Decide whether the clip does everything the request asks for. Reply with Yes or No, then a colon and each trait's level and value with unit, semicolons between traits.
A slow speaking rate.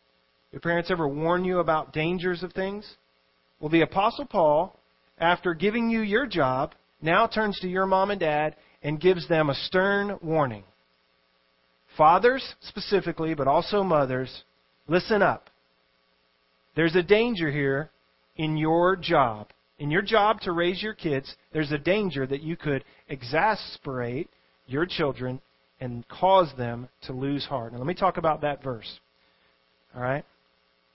No: average, 145 wpm